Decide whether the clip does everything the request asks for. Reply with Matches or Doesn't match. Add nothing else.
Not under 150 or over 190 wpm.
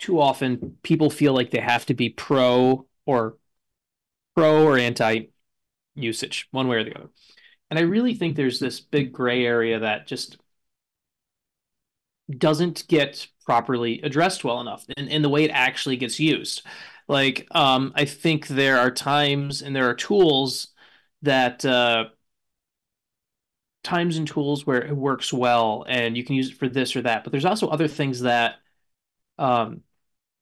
Matches